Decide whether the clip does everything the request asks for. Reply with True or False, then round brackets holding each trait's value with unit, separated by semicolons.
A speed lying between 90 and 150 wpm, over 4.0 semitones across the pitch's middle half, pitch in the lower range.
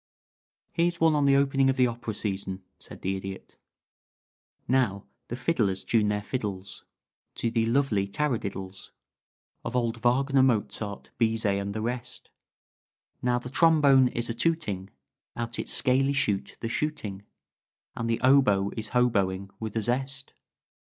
True (145 wpm; 4.8 semitones; 115 Hz)